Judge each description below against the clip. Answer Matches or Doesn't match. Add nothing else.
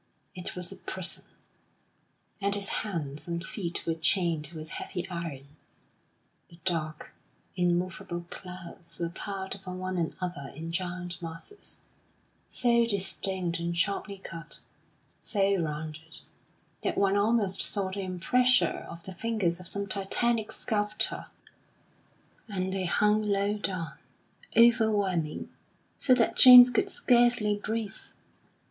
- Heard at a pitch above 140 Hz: Matches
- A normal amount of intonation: Matches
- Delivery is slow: Matches